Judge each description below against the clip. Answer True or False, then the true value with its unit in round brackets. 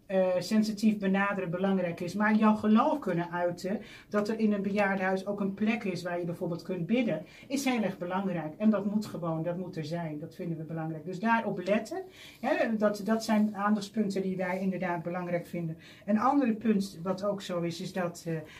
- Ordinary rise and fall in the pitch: True (3.3 semitones)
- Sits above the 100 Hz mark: True (190 Hz)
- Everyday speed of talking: False (205 wpm)